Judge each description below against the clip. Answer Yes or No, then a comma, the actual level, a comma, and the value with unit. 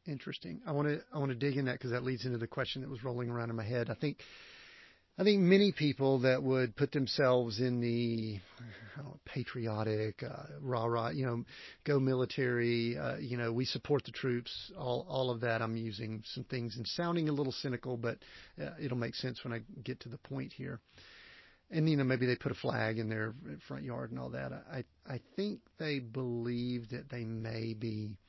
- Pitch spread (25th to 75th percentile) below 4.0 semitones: Yes, average, 3.2 semitones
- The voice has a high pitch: No, low, 125 Hz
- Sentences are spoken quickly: Yes, fast, 210 wpm